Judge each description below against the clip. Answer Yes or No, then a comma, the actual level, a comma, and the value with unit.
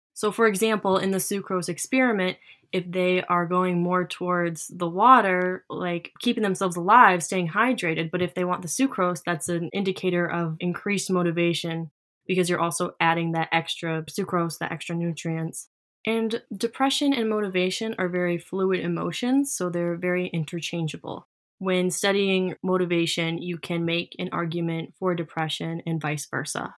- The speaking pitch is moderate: Yes, medium, 180 Hz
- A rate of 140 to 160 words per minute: Yes, average, 150 wpm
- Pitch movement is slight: Yes, narrow, 2.1 semitones